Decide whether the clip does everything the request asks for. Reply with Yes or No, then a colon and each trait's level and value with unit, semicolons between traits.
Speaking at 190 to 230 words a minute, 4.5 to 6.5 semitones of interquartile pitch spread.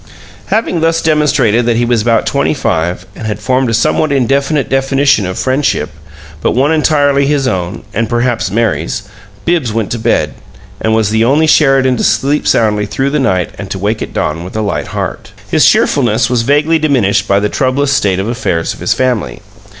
Yes: average, 195 wpm; average, 4.9 semitones